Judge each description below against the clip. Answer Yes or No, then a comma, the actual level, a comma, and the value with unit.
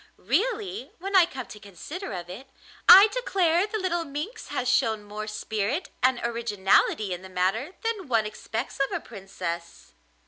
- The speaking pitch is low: No, high, 245 Hz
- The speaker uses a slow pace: No, average, 165 wpm